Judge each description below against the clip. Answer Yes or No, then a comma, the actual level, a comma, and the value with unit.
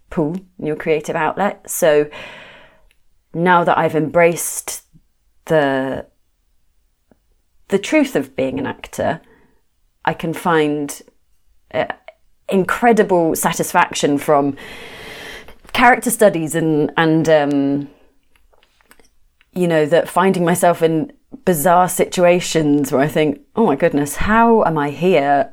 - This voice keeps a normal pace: No, slow, 110 wpm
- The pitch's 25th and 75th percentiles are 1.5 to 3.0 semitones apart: No, average, 4.3 semitones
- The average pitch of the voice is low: No, medium, 165 Hz